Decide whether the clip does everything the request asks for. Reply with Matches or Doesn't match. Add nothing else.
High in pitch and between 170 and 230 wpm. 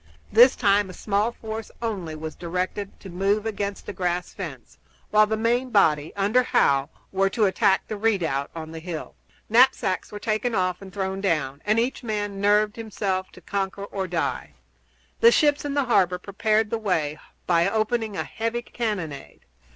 Matches